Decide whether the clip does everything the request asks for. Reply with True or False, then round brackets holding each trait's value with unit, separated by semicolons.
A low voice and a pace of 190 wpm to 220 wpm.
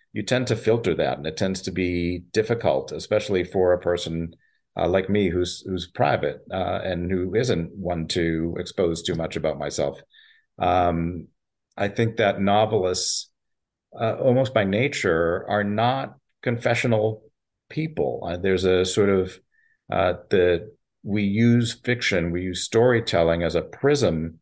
False (95 Hz; 150 wpm)